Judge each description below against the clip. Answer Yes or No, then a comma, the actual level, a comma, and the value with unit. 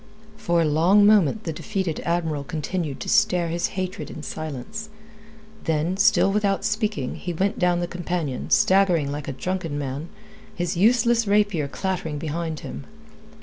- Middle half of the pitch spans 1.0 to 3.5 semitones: No, average, 4.1 semitones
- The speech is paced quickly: No, average, 150 wpm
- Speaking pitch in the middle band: Yes, medium, 175 Hz